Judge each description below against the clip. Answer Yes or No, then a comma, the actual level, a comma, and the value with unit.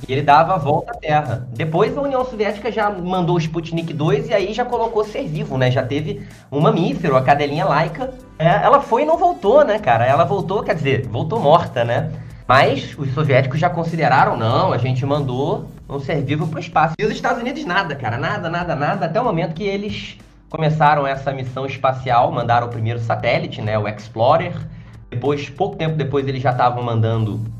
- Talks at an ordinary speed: No, fast, 205 wpm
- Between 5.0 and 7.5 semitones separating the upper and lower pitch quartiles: Yes, wide, 5.5 semitones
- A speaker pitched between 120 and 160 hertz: Yes, medium, 150 Hz